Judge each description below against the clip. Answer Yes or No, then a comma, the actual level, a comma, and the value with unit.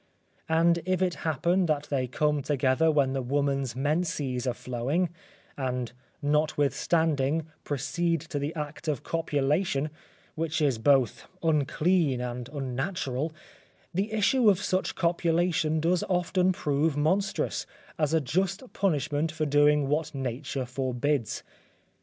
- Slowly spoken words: Yes, slow, 125 wpm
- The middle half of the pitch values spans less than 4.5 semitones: Yes, average, 3.6 semitones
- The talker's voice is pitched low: No, medium, 150 Hz